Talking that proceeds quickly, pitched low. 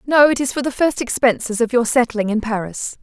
No: fast, 240 wpm; high, 240 Hz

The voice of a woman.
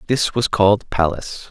No: male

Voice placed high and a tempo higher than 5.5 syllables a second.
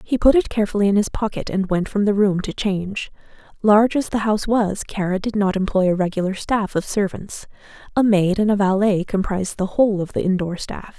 Yes: high, 200 Hz; 5.8 syllables/s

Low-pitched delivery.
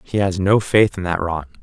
Yes: very low, 95 Hz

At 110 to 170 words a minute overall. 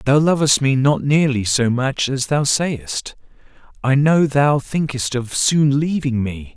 Yes: average, 165 wpm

